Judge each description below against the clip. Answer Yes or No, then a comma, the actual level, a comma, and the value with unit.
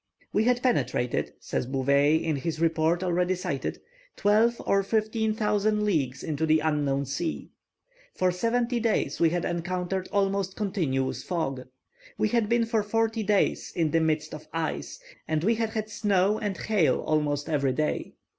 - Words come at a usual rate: Yes, average, 160 wpm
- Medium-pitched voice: Yes, medium, 180 Hz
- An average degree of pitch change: No, wide, 5.7 semitones